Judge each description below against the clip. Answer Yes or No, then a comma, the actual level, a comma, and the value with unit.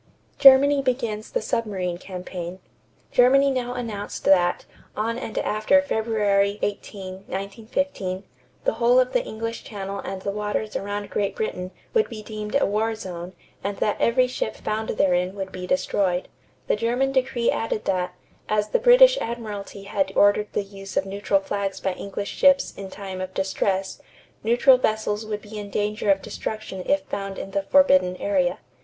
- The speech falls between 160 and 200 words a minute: Yes, average, 165 wpm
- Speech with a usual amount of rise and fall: Yes, average, 3.3 semitones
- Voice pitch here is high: Yes, high, 210 Hz